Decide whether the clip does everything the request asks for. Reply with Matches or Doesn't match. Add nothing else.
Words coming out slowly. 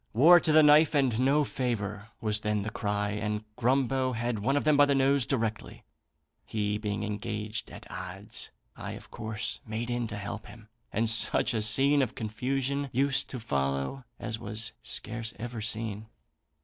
Doesn't match